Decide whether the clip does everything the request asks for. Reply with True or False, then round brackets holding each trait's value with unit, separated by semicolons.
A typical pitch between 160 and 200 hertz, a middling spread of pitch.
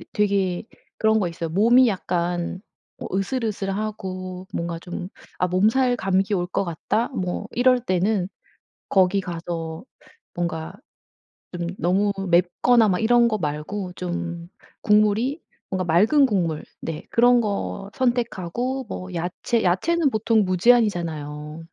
True (190 Hz; 4.1 semitones)